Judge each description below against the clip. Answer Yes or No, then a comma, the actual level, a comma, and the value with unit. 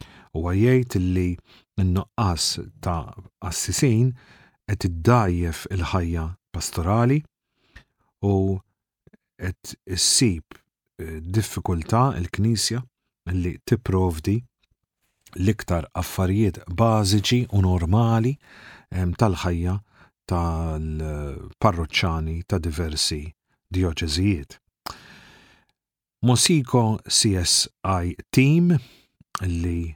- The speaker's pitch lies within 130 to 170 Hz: No, very low, 95 Hz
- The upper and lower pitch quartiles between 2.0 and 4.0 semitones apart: No, average, 4.7 semitones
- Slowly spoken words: Yes, slow, 60 wpm